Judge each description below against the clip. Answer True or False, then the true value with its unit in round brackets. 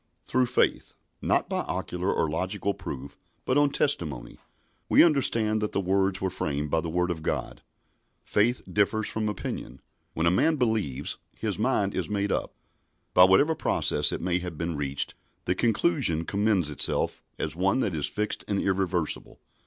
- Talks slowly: False (170 wpm)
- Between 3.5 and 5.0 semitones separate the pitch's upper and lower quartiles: True (4.4 semitones)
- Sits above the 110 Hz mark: False (95 Hz)